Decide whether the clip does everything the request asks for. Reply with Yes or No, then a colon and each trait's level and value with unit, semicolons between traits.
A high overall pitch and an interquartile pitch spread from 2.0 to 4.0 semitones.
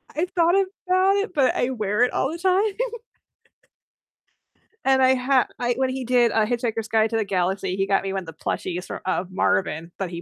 No: high, 240 Hz; wide, 5.6 semitones